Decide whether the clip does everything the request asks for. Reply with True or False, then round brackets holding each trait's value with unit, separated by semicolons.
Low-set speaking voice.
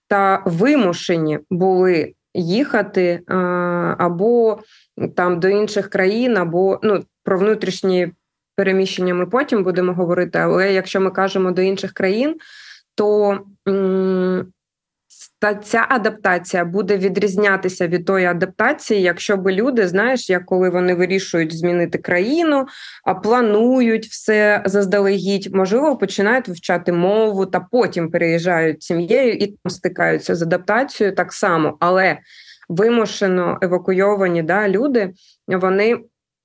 False (190 Hz)